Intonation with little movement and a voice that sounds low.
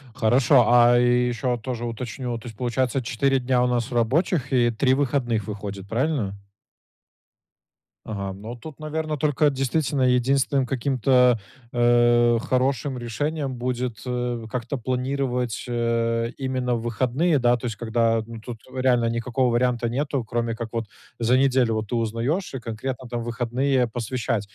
Yes: narrow, 2.1 semitones; low, 125 Hz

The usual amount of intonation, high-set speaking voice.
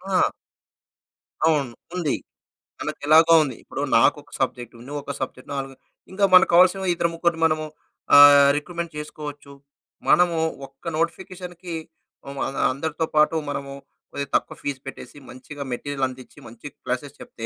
No: average, 3.4 semitones; medium, 145 Hz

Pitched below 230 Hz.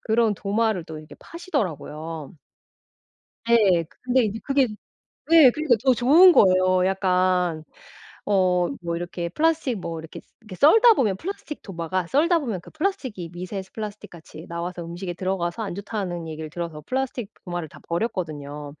Yes: medium, 185 Hz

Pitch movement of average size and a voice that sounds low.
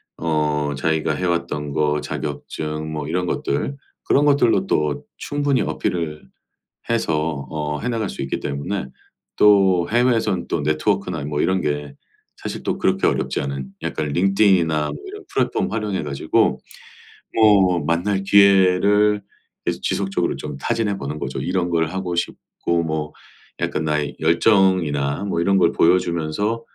Yes: average, 4.8 semitones; very low, 85 Hz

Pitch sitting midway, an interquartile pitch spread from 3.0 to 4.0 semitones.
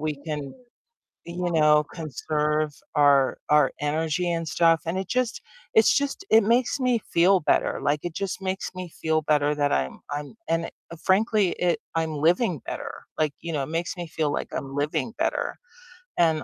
Yes: medium, 160 Hz; average, 3.4 semitones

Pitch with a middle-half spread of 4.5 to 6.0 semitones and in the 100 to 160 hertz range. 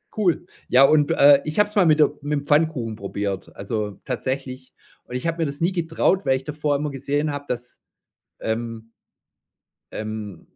Yes: average, 4.8 semitones; medium, 140 Hz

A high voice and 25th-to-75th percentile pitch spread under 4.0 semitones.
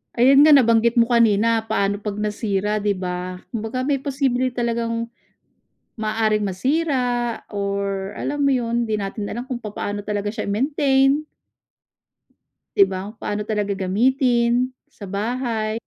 Yes: high, 225 Hz; average, 3.5 semitones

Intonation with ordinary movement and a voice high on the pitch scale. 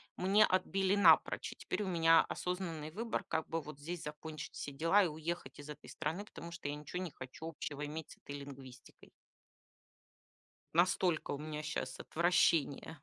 No: average, 3.1 semitones; medium, 160 Hz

